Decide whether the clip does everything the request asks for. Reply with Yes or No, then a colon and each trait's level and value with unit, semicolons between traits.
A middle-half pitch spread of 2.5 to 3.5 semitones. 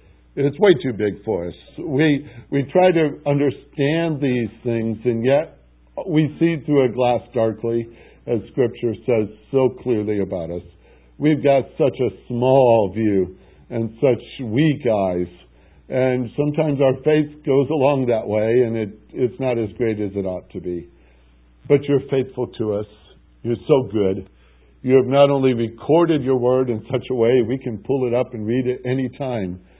No: average, 4.6 semitones